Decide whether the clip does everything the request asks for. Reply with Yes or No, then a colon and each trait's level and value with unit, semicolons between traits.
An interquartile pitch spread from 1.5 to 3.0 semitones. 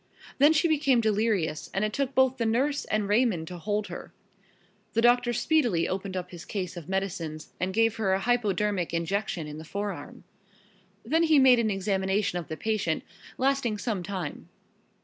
No: average, 4.8 semitones